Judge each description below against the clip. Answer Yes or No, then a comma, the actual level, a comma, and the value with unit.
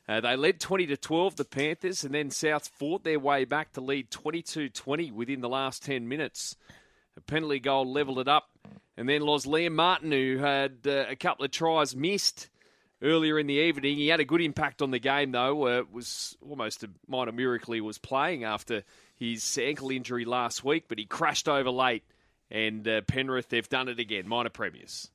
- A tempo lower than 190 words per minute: No, fast, 205 wpm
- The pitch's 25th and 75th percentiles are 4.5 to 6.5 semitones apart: No, average, 3.1 semitones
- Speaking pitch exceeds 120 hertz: Yes, medium, 140 Hz